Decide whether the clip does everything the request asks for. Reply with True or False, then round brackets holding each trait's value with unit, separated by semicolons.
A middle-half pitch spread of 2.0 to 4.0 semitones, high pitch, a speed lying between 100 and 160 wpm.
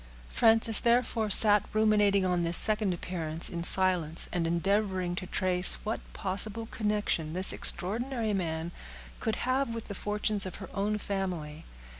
True (3.4 semitones; 195 Hz; 145 wpm)